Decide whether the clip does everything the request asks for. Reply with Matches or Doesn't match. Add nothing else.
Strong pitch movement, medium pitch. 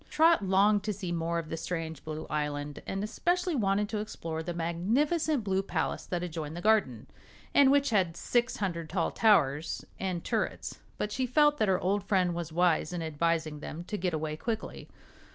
Doesn't match